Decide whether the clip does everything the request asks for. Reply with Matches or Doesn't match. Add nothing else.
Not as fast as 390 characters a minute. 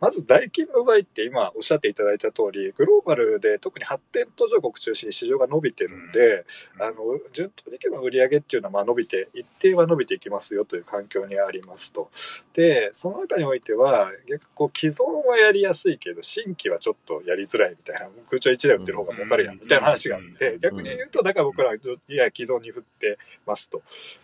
Doesn't match